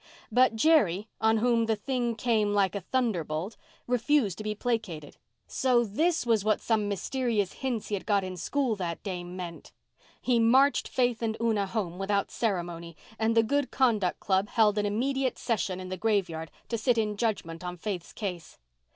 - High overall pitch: Yes, high, 215 Hz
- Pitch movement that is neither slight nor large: Yes, average, 4.1 semitones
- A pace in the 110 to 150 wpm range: No, average, 175 wpm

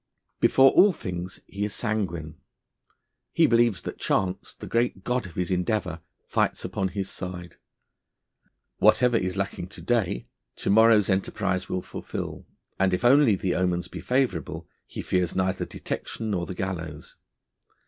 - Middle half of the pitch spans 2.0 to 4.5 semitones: Yes, average, 3.6 semitones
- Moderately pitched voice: No, very low, 95 Hz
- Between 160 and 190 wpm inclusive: No, average, 150 wpm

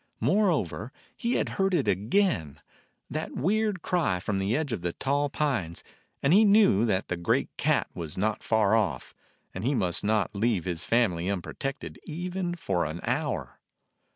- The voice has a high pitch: No, low, 115 Hz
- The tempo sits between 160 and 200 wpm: Yes, average, 165 wpm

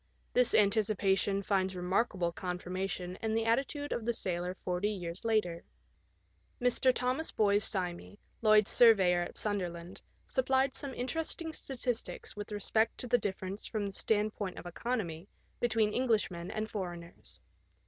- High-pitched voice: Yes, high, 205 Hz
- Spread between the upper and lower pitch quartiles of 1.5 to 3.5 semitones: No, average, 4.1 semitones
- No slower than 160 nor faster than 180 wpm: No, average, 140 wpm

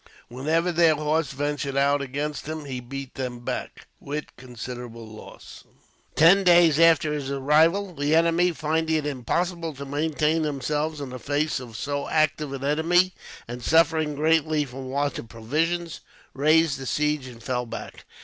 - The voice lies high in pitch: No, medium, 150 Hz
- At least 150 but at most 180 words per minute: Yes, average, 160 wpm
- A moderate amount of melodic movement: Yes, average, 3.0 semitones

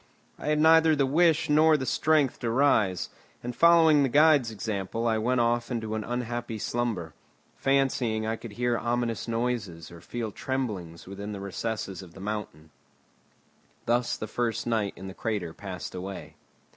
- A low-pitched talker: Yes, low, 115 Hz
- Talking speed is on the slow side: No, average, 165 wpm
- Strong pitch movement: No, average, 4.4 semitones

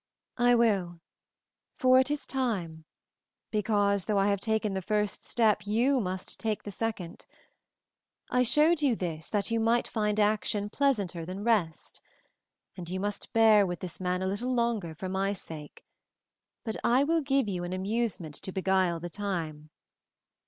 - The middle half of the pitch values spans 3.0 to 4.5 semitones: Yes, average, 4.0 semitones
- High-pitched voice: Yes, high, 205 Hz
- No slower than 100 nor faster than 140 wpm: No, average, 160 wpm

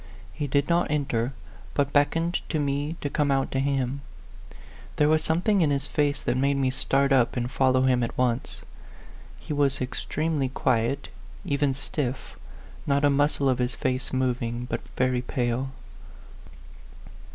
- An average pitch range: No, narrow, 2.2 semitones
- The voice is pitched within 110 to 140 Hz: Yes, low, 135 Hz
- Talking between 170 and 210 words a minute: No, average, 160 wpm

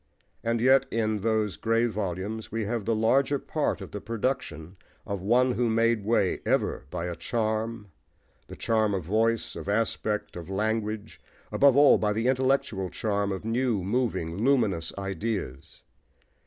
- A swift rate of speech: No, average, 155 wpm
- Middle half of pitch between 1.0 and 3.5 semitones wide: Yes, average, 2.7 semitones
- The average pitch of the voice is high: No, low, 110 Hz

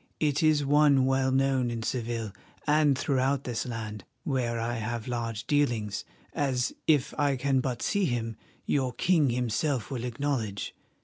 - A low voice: Yes, low, 130 Hz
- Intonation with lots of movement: No, average, 3.3 semitones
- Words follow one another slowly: No, average, 150 wpm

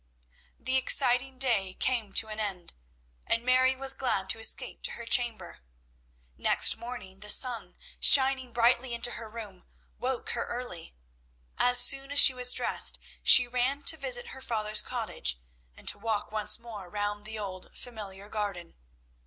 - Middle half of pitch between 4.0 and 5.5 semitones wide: No, average, 3.5 semitones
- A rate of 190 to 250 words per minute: No, average, 160 wpm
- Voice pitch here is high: Yes, high, 235 Hz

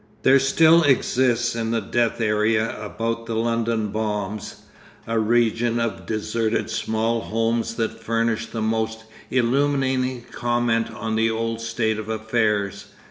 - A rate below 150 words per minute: Yes, slow, 135 wpm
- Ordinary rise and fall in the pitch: No, narrow, 1.2 semitones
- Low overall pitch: Yes, low, 115 Hz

